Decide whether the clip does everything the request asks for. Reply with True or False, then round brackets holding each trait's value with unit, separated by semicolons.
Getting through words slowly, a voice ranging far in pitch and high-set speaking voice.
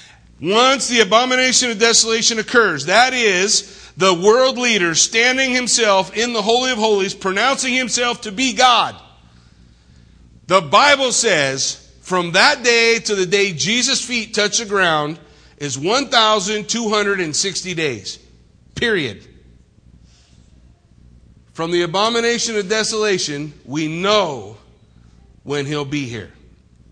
True (115 wpm; 7.7 semitones; 200 Hz)